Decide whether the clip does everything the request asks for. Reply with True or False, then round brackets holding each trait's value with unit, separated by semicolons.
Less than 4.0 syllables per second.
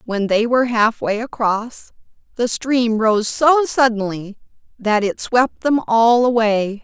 True (3.8 syllables/s)